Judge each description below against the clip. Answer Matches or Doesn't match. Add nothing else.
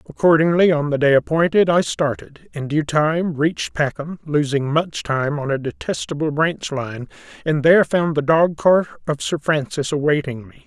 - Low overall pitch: Doesn't match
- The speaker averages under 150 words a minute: Doesn't match